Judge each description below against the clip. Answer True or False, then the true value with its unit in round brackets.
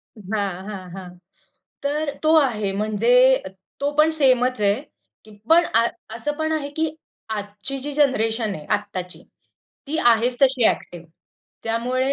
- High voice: True (240 Hz)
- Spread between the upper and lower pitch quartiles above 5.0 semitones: True (5.4 semitones)